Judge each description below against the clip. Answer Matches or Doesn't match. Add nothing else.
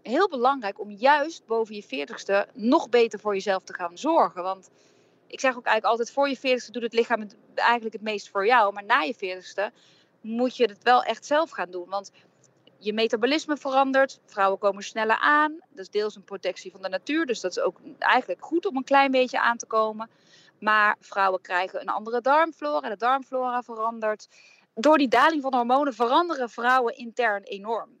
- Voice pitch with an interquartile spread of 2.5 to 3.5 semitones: Doesn't match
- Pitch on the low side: Doesn't match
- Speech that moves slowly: Doesn't match